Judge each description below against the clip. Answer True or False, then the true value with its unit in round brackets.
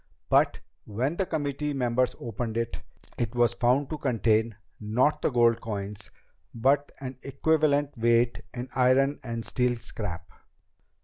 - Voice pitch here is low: True (120 Hz)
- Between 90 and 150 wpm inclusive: True (135 wpm)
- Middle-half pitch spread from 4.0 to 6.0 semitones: False (3.2 semitones)